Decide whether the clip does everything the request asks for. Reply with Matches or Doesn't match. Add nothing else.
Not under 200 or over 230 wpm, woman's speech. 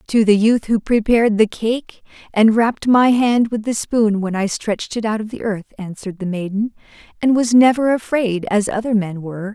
Matches